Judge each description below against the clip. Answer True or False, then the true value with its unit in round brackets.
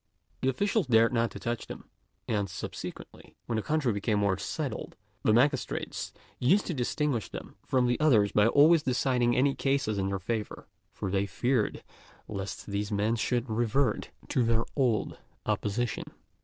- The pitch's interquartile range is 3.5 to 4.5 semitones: True (4.1 semitones)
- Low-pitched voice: True (120 Hz)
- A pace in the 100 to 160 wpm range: True (155 wpm)